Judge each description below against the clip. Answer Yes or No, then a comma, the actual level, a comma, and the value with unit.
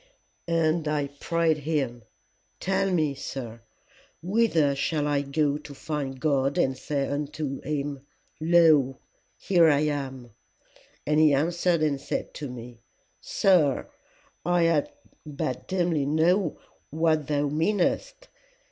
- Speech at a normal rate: No, slow, 120 wpm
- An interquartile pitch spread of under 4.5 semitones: Yes, average, 3.1 semitones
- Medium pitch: Yes, medium, 150 Hz